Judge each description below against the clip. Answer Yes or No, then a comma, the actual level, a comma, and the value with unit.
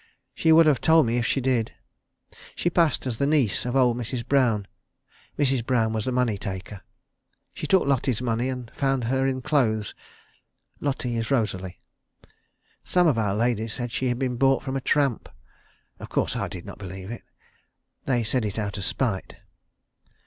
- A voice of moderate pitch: No, low, 125 Hz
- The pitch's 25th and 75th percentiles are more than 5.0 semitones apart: No, average, 3.4 semitones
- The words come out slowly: No, average, 180 wpm